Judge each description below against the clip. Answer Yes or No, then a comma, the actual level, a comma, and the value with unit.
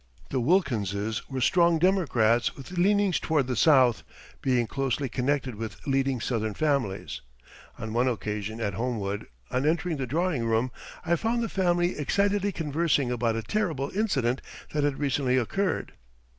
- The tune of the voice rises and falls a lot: Yes, wide, 6.4 semitones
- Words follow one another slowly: No, average, 150 wpm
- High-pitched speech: No, low, 135 Hz